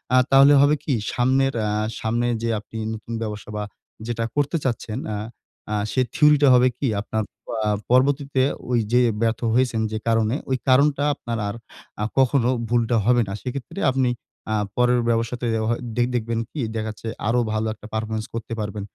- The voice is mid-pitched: No, low, 120 Hz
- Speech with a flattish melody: No, average, 3.1 semitones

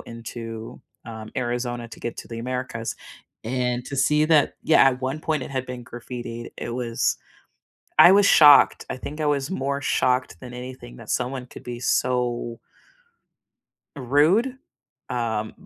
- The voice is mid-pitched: No, low, 125 Hz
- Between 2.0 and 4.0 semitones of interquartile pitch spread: Yes, average, 2.7 semitones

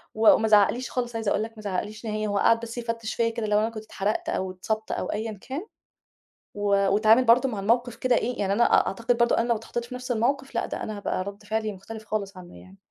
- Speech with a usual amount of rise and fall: No, narrow, 2.3 semitones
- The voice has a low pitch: No, high, 220 Hz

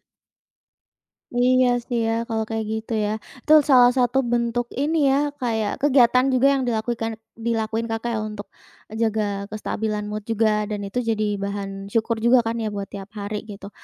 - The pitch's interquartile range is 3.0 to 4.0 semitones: No, narrow, 2.4 semitones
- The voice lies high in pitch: Yes, high, 225 Hz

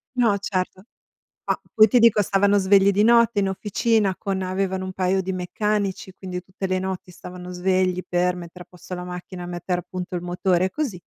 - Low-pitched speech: No, medium, 185 Hz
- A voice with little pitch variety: Yes, narrow, 1.9 semitones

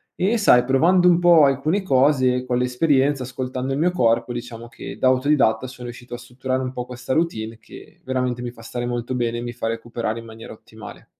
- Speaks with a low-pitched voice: Yes, low, 125 Hz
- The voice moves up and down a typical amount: No, narrow, 2.2 semitones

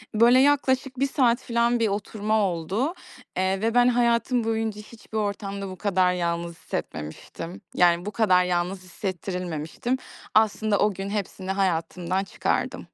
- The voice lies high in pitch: Yes, high, 200 Hz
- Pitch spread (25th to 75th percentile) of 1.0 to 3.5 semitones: No, average, 4.3 semitones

